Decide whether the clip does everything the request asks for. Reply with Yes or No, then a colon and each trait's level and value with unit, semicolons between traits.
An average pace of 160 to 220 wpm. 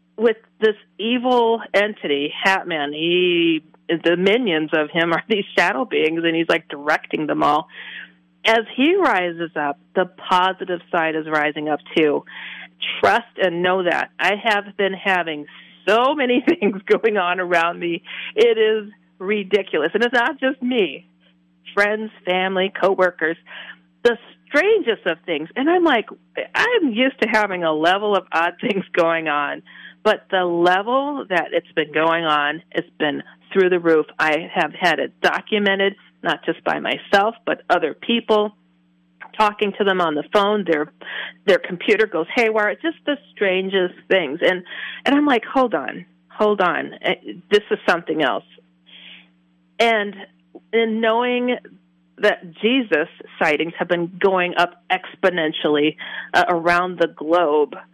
No: average, 150 wpm